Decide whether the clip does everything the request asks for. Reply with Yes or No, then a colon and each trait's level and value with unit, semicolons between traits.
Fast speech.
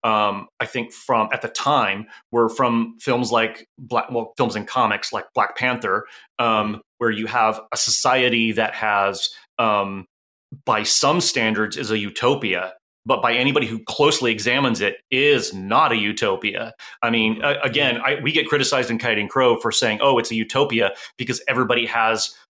No: average, 175 wpm